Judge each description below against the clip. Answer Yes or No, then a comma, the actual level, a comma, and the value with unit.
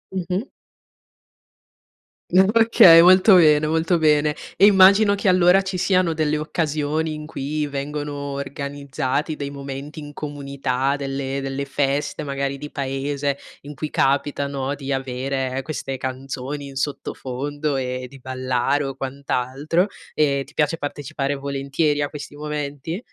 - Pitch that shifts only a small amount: Yes, narrow, 2.1 semitones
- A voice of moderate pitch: Yes, medium, 145 Hz